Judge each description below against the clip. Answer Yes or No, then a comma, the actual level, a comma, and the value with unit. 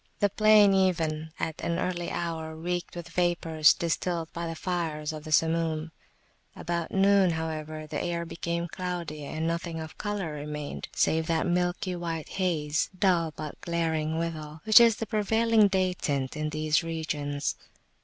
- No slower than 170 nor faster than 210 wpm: No, average, 155 wpm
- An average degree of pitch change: No, narrow, 2.3 semitones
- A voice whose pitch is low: No, medium, 165 Hz